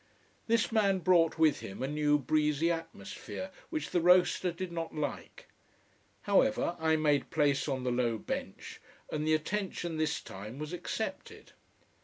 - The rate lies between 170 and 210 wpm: No, average, 150 wpm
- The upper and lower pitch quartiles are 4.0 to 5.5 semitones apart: No, average, 3.5 semitones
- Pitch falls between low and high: Yes, medium, 160 Hz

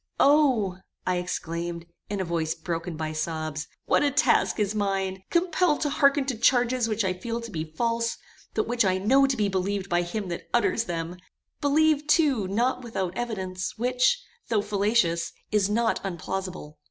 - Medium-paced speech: Yes, average, 170 wpm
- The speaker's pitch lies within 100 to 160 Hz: No, high, 205 Hz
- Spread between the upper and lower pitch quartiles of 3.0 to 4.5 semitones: No, wide, 5.4 semitones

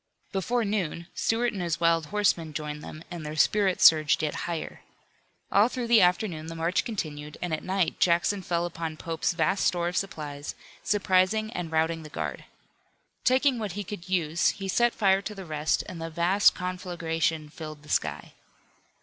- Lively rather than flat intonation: No, average, 3.6 semitones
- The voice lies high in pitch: No, medium, 175 Hz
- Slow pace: No, average, 175 wpm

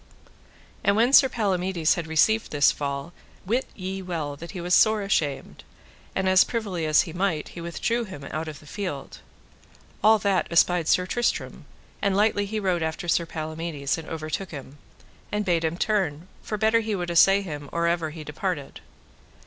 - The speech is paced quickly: No, average, 180 wpm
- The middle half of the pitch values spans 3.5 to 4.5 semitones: Yes, average, 4.2 semitones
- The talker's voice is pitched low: No, medium, 175 Hz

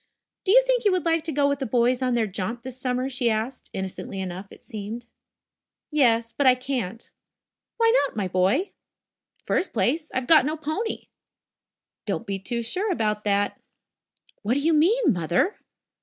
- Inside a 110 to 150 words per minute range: No, average, 175 wpm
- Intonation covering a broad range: Yes, wide, 6.3 semitones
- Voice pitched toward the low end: No, very high, 250 Hz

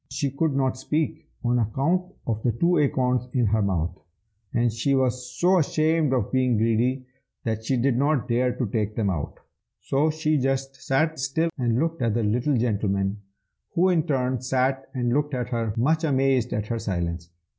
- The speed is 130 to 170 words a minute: No, average, 185 wpm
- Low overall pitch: Yes, low, 130 Hz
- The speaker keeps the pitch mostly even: No, average, 3.7 semitones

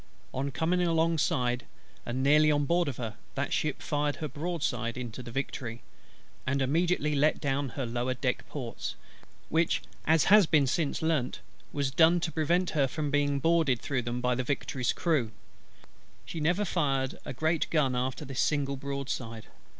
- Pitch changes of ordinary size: Yes, average, 3.9 semitones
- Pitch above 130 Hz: Yes, medium, 140 Hz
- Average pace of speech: Yes, average, 165 wpm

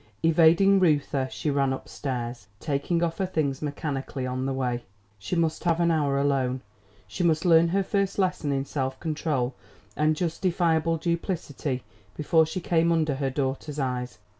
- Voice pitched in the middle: Yes, medium, 150 Hz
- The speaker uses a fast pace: No, average, 165 wpm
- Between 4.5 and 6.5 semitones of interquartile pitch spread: No, average, 3.9 semitones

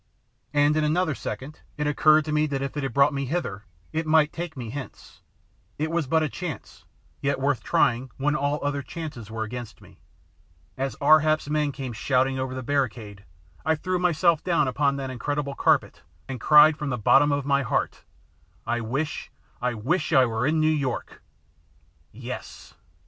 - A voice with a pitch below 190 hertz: Yes, medium, 140 Hz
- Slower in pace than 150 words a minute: No, average, 180 wpm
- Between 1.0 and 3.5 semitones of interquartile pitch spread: Yes, average, 3.0 semitones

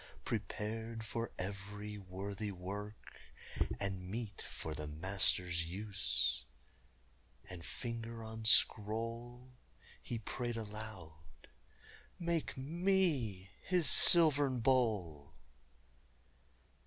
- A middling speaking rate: No, slow, 80 wpm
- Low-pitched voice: Yes, low, 105 Hz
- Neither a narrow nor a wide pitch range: Yes, average, 4.0 semitones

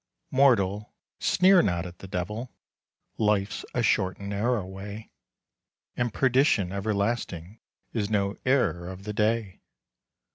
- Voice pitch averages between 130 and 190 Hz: No, low, 105 Hz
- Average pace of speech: No, slow, 120 wpm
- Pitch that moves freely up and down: No, average, 3.4 semitones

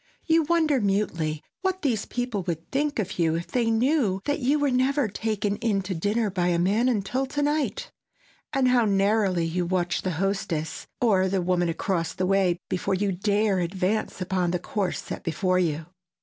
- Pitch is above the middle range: Yes, high, 200 Hz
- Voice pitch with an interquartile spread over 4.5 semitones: Yes, wide, 5.4 semitones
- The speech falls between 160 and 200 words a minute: Yes, average, 185 wpm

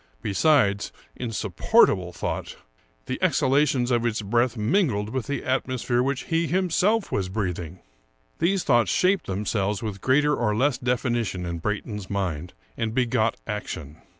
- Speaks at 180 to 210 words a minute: No, average, 150 wpm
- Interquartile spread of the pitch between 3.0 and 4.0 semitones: No, average, 5.0 semitones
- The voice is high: No, low, 115 Hz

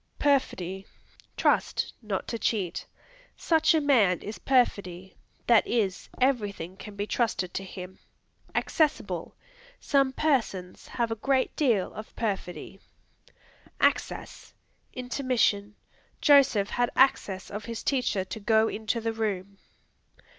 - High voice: Yes, high, 220 Hz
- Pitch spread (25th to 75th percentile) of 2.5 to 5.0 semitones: Yes, average, 4.7 semitones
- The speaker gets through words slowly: Yes, slow, 120 wpm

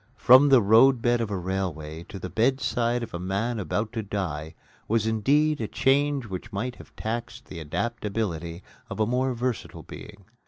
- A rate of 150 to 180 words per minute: Yes, average, 170 wpm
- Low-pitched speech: Yes, low, 110 Hz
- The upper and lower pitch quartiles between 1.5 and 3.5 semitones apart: No, average, 4.1 semitones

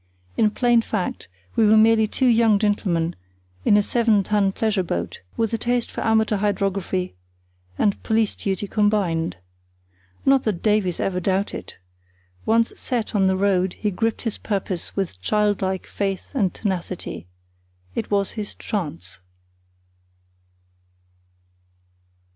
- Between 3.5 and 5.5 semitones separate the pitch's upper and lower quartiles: No, average, 2.7 semitones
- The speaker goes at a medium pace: No, slow, 130 wpm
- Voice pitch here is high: Yes, high, 205 Hz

